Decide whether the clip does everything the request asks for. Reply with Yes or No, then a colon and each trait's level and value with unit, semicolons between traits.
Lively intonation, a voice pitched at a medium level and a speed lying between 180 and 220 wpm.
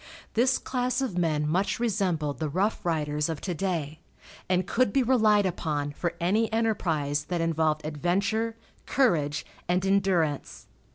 No: wide, 5.8 semitones; medium, 180 Hz; average, 140 wpm